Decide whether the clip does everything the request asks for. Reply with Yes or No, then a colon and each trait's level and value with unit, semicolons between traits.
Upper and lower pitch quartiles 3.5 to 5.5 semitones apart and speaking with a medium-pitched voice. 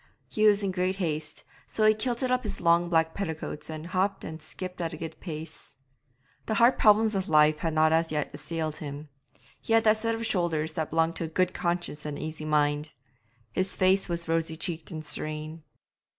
Yes: average, 3.8 semitones; medium, 165 Hz